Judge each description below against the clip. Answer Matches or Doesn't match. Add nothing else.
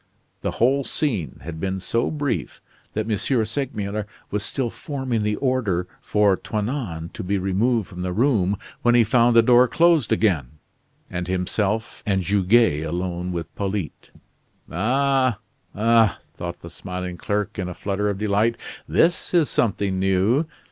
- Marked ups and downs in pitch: Doesn't match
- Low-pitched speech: Matches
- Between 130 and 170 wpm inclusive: Matches